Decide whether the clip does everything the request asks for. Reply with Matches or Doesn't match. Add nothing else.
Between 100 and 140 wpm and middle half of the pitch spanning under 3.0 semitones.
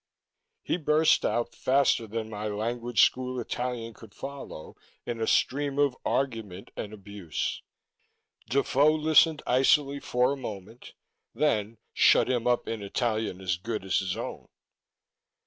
Doesn't match